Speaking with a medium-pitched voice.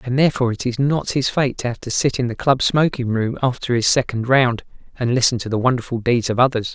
No: low, 125 Hz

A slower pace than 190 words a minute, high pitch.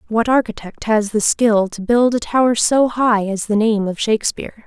No: fast, 205 wpm; high, 220 Hz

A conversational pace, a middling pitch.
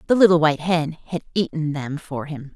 No: fast, 210 wpm; medium, 160 Hz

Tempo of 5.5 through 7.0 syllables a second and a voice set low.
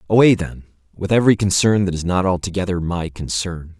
Yes: 5.7 syllables/s; very low, 90 Hz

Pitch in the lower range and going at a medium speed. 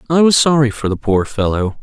No: low, 125 Hz; fast, 230 wpm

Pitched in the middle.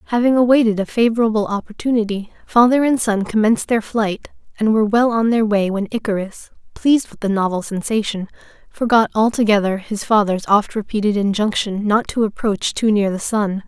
No: high, 215 Hz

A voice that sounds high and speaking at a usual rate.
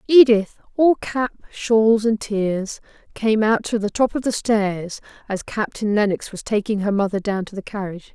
Yes: high, 215 Hz; average, 185 wpm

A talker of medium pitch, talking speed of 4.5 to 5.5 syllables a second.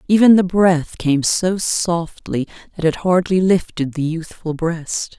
No: medium, 170 Hz; 3.8 syllables/s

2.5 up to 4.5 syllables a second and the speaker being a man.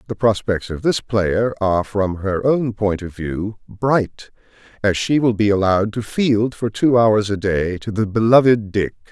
Yes: 4.3 syllables/s; male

